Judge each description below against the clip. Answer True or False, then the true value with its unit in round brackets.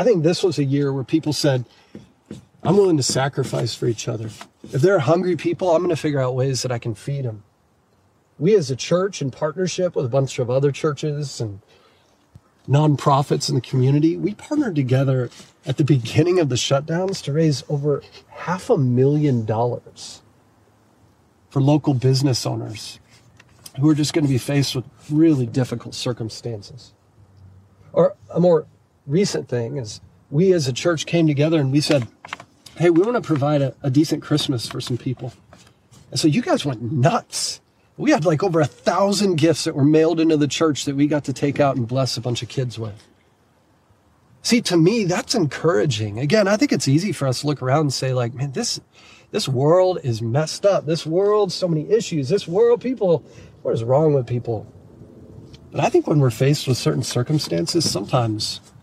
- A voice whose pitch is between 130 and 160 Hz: True (140 Hz)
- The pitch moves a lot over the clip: False (5.0 semitones)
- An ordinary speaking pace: True (190 wpm)